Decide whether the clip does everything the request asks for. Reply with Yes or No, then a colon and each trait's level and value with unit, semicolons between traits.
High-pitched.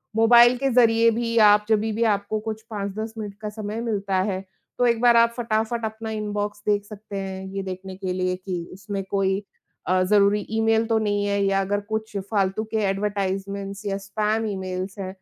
Yes: high, 205 Hz